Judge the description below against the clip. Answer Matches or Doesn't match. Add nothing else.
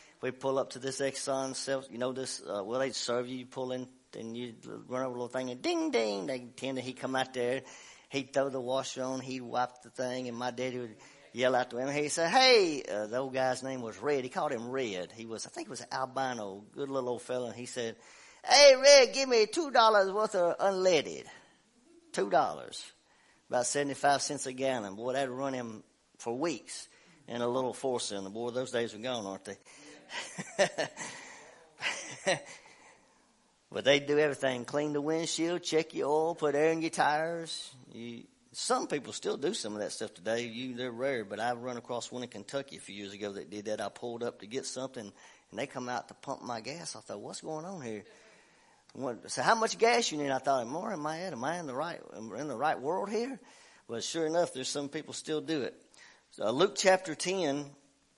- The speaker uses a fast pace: Matches